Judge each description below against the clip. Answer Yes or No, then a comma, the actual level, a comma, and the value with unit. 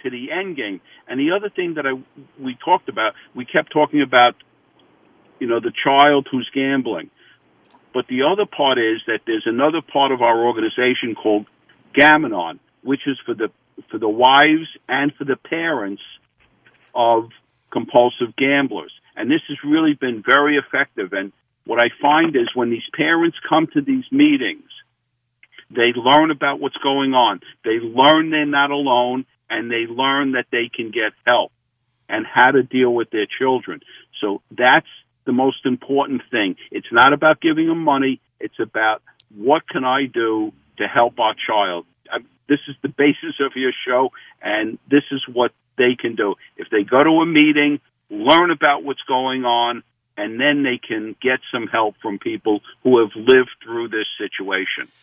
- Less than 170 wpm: No, average, 175 wpm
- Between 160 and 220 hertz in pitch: No, low, 135 Hz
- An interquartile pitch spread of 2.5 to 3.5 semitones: No, average, 4.1 semitones